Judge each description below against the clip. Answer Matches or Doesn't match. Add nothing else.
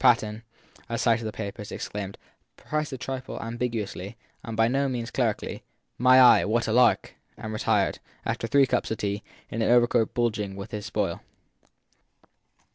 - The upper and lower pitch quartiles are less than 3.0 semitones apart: Matches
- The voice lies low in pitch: Matches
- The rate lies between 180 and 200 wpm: Doesn't match